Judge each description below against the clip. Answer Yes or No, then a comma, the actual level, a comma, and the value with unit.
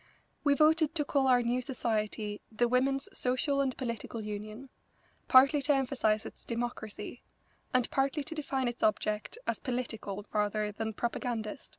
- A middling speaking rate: Yes, average, 150 wpm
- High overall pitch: Yes, high, 245 Hz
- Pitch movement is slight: No, average, 4.0 semitones